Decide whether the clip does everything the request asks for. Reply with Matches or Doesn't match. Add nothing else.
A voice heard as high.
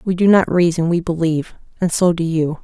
Doesn't match